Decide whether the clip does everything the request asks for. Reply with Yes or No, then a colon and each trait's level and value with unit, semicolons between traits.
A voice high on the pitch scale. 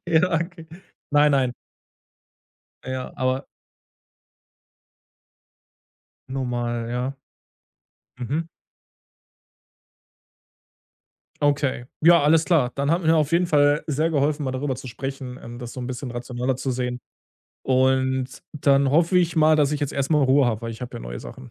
No: low, 135 Hz